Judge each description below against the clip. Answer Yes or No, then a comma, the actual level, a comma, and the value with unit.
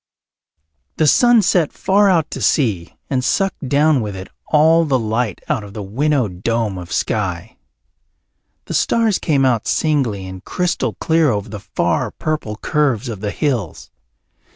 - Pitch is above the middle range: No, low, 130 Hz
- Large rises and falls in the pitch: Yes, wide, 7.0 semitones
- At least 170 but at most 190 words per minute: No, average, 155 wpm